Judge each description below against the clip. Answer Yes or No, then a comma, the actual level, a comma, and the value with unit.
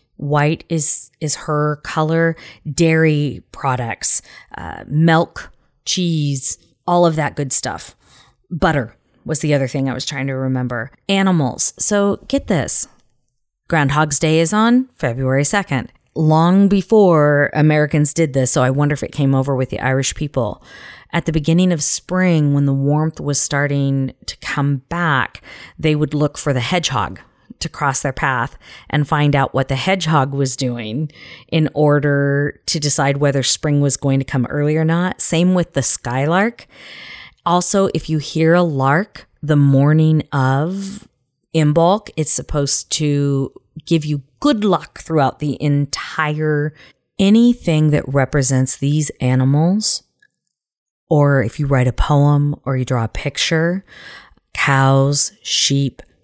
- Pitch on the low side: No, medium, 150 Hz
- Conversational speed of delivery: Yes, average, 145 wpm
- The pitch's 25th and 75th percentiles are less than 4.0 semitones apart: Yes, average, 3.3 semitones